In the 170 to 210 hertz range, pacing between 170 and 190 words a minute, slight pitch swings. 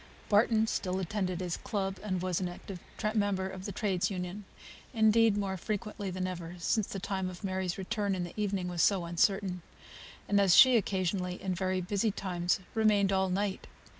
Yes: high, 190 Hz; average, 180 wpm; narrow, 2.1 semitones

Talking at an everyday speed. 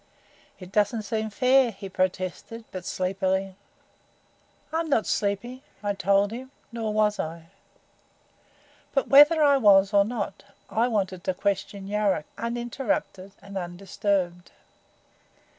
No: slow, 120 wpm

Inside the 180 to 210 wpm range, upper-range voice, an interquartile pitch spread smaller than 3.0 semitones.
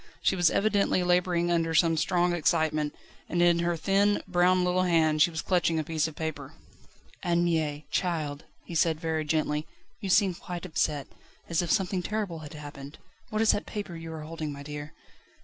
No: average, 185 wpm; medium, 165 Hz; narrow, 2.5 semitones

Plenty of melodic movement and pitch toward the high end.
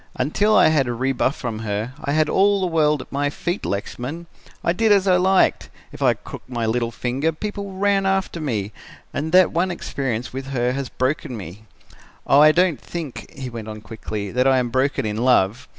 No: wide, 6.2 semitones; low, 135 Hz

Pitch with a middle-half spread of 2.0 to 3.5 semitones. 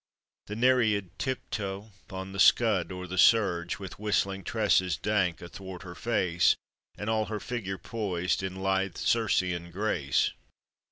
Yes: average, 2.7 semitones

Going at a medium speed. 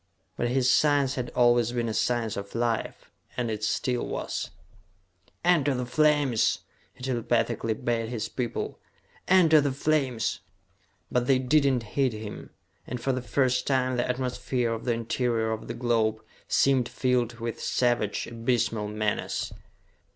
Yes: average, 150 wpm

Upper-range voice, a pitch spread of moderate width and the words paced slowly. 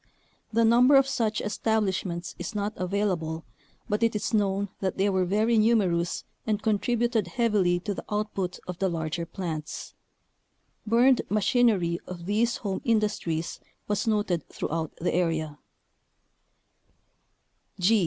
Yes: high, 200 Hz; average, 3.9 semitones; slow, 130 wpm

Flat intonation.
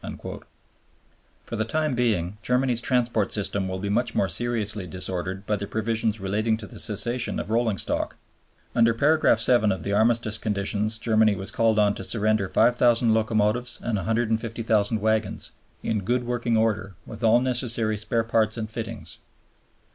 Yes: narrow, 2.2 semitones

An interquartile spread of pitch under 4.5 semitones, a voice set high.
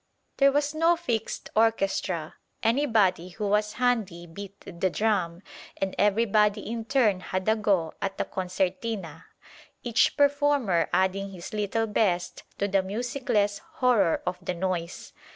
Yes: average, 3.6 semitones; high, 205 Hz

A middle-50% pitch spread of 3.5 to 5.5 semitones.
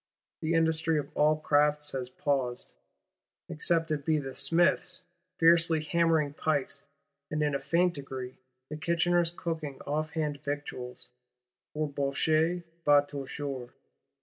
No: narrow, 2.5 semitones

